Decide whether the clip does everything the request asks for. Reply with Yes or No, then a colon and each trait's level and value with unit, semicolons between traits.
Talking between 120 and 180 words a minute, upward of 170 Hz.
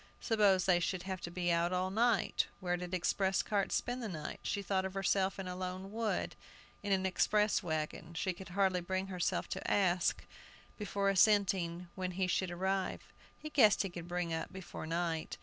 No: average, 190 wpm; medium, 185 Hz